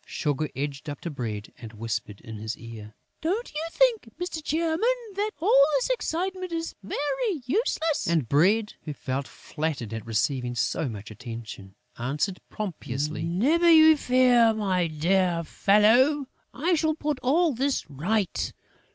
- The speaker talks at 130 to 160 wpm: Yes, average, 145 wpm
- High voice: Yes, high, 195 Hz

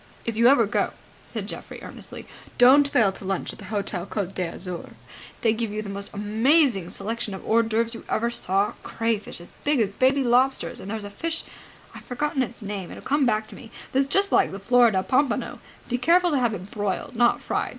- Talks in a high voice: Yes, high, 225 Hz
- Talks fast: Yes, fast, 210 wpm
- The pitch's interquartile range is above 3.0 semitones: Yes, average, 4.2 semitones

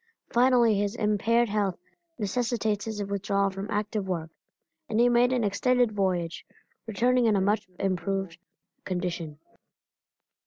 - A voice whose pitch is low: No, high, 205 Hz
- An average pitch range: Yes, average, 3.1 semitones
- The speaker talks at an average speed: No, slow, 125 wpm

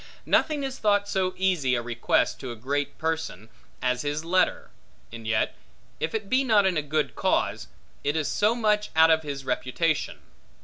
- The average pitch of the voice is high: No, medium, 160 Hz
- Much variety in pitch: Yes, wide, 7.2 semitones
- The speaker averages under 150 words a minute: No, average, 180 wpm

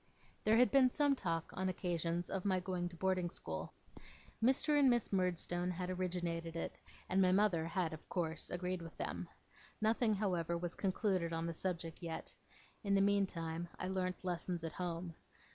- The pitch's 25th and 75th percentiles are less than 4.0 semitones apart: Yes, narrow, 2.5 semitones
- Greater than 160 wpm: Yes, average, 175 wpm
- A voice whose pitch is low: No, medium, 180 Hz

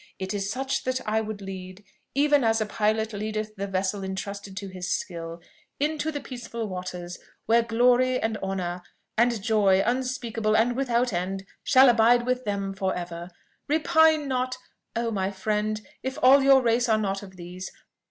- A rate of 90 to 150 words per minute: No, average, 170 wpm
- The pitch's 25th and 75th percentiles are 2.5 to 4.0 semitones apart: No, average, 4.5 semitones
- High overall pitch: Yes, high, 215 Hz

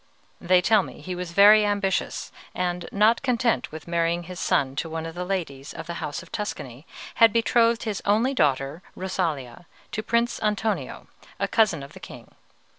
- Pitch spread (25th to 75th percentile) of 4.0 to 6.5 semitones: Yes, average, 4.8 semitones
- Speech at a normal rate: Yes, average, 180 wpm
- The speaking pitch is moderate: Yes, medium, 180 Hz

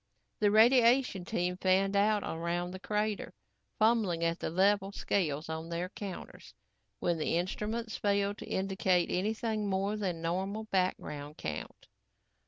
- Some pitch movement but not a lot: Yes, average, 3.3 semitones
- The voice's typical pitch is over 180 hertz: Yes, high, 190 Hz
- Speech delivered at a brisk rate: No, slow, 135 wpm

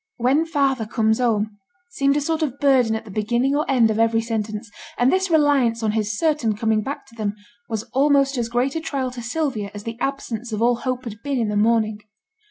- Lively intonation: No, average, 3.9 semitones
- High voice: Yes, high, 240 Hz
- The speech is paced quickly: Yes, fast, 220 wpm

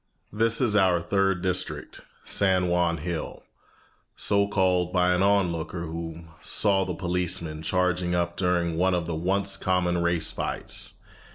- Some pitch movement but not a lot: No, narrow, 2.0 semitones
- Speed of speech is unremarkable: Yes, average, 150 wpm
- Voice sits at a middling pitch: No, very low, 90 Hz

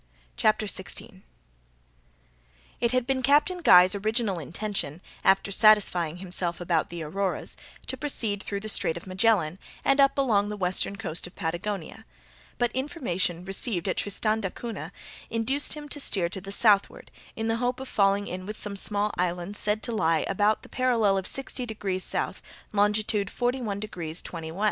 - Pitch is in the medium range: No, high, 205 Hz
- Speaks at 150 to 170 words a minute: Yes, average, 165 wpm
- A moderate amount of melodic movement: Yes, average, 3.7 semitones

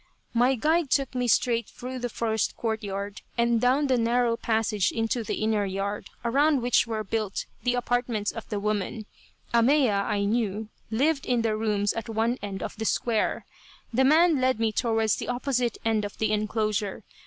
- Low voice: No, high, 225 Hz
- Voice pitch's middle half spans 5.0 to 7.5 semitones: No, narrow, 2.6 semitones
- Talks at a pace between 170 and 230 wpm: Yes, average, 180 wpm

